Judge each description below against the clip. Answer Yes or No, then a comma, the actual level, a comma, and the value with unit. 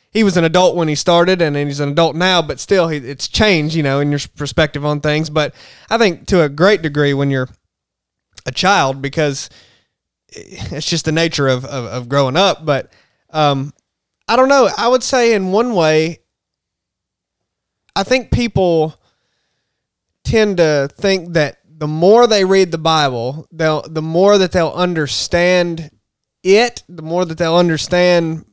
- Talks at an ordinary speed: Yes, average, 170 wpm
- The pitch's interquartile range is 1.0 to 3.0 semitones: No, average, 4.0 semitones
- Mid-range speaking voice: Yes, medium, 160 Hz